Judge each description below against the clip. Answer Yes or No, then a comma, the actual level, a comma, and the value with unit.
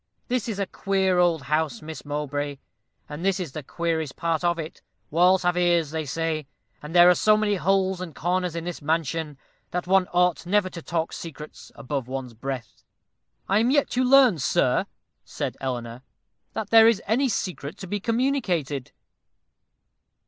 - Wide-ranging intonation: No, average, 4.3 semitones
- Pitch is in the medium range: Yes, medium, 170 Hz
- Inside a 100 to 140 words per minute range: No, average, 170 wpm